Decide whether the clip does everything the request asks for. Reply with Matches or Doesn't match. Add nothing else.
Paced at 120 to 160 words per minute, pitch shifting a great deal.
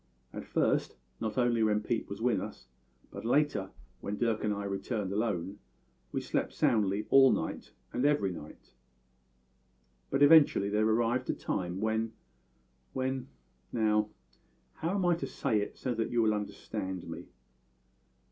Doesn't match